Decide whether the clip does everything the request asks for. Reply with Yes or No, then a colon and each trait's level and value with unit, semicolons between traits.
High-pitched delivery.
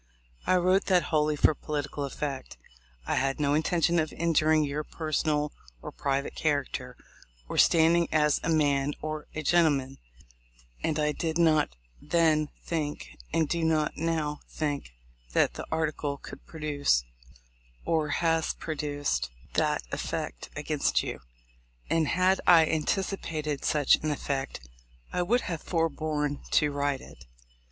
No: medium, 155 Hz